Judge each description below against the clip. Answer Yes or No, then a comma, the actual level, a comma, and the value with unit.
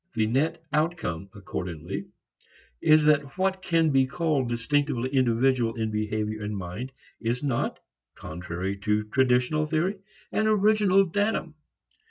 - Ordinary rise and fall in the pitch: No, wide, 6.8 semitones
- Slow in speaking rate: Yes, slow, 125 wpm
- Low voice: Yes, low, 130 Hz